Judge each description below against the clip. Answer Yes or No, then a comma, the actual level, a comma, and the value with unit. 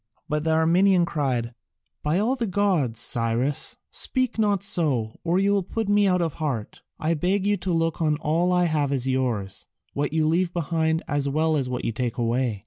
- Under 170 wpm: No, average, 200 wpm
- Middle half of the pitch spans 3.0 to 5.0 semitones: No, wide, 5.4 semitones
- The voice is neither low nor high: Yes, medium, 160 Hz